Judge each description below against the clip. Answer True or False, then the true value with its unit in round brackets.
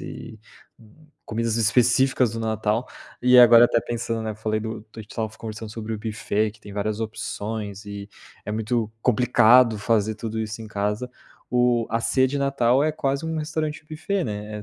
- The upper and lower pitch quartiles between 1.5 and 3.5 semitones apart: True (2.5 semitones)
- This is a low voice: True (115 Hz)